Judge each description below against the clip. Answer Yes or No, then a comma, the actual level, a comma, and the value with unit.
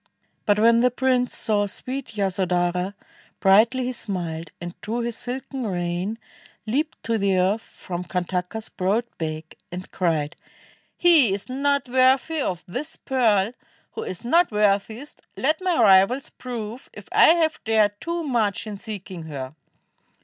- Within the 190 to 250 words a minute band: No, average, 145 wpm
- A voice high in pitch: Yes, high, 215 Hz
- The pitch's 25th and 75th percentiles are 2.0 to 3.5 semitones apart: No, wide, 5.5 semitones